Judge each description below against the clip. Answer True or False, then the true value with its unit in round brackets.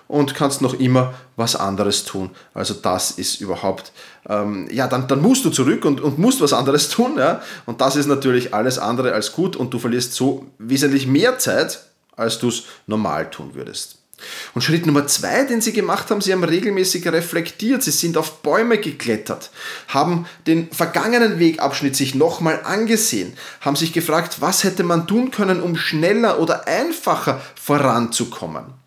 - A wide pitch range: True (5.9 semitones)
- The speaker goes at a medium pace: True (175 wpm)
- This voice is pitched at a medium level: True (145 Hz)